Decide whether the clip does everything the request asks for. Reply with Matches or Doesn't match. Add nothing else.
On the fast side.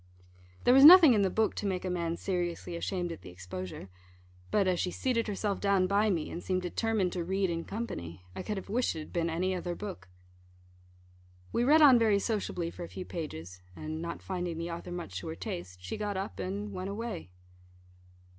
Matches